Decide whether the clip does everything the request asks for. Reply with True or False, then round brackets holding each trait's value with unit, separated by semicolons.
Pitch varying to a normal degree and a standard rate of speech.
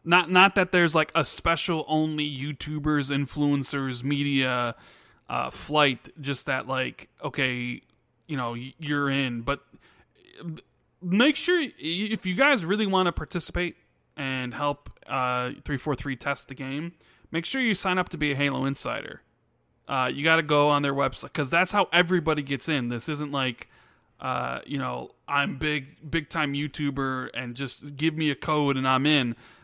True (3.5 semitones; 170 wpm)